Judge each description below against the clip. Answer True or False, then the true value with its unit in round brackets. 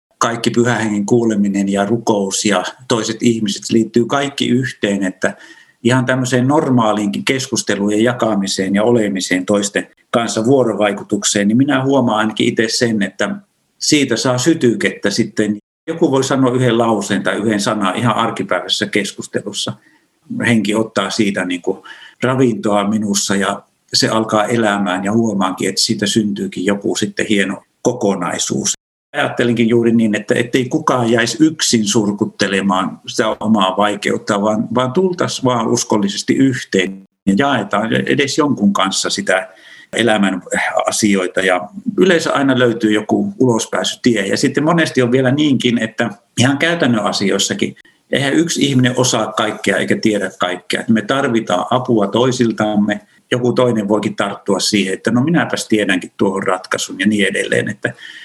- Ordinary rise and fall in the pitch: True (3.4 semitones)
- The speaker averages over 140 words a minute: False (135 wpm)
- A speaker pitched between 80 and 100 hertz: False (110 Hz)